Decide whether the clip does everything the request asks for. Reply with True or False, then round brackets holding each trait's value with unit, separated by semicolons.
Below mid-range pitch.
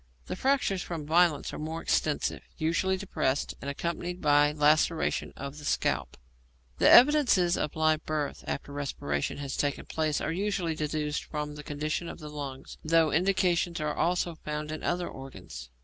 False (155 Hz)